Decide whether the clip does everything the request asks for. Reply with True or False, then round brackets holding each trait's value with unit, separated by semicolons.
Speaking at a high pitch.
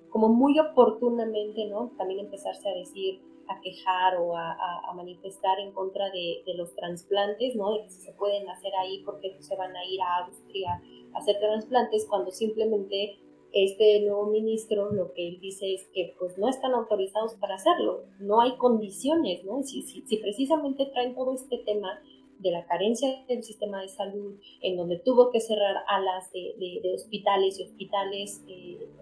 True (205 Hz)